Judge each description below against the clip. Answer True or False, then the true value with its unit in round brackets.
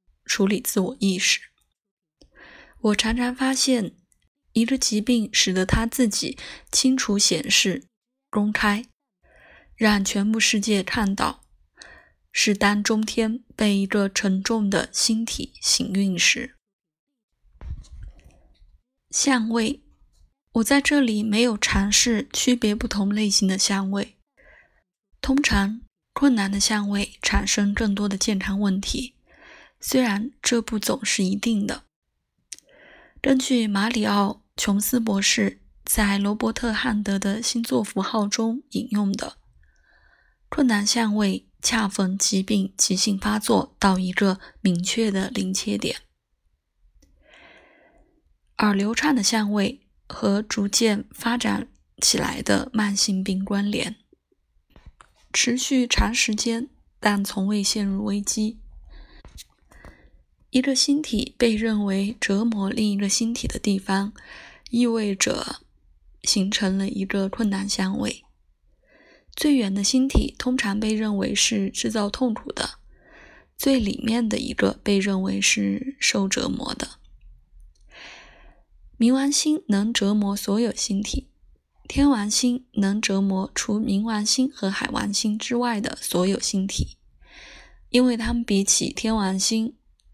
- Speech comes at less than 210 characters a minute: True (180 characters per minute)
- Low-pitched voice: False (215 Hz)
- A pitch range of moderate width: True (3.1 semitones)